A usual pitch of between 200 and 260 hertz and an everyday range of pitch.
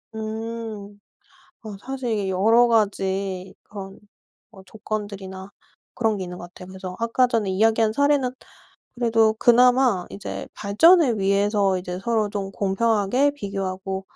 Yes: high, 210 Hz; average, 3.1 semitones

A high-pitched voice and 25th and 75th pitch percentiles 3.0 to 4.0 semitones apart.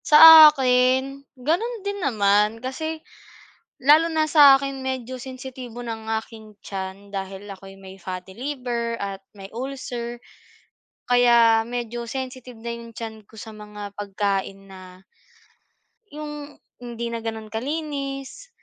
No: high, 235 Hz; average, 4.5 semitones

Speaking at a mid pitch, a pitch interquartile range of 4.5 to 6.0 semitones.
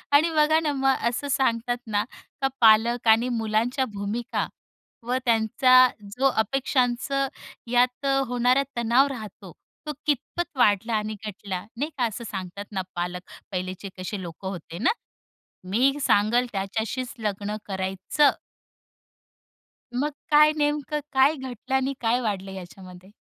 No: high, 235 Hz; average, 4.8 semitones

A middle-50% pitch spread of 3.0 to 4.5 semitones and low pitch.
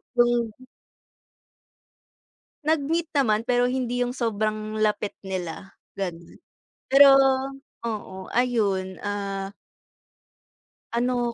No: average, 3.9 semitones; high, 225 Hz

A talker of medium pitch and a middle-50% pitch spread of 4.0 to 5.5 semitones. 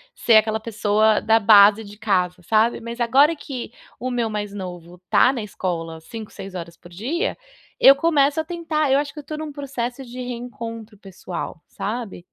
No: high, 225 Hz; average, 4.8 semitones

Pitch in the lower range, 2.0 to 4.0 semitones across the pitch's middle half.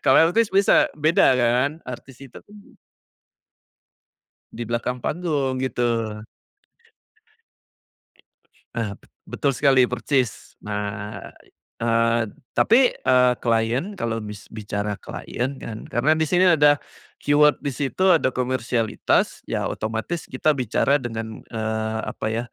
No: low, 125 Hz; average, 4.7 semitones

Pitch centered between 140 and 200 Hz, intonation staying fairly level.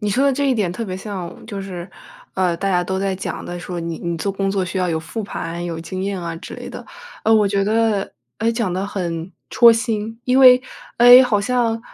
No: high, 195 Hz; average, 4.1 semitones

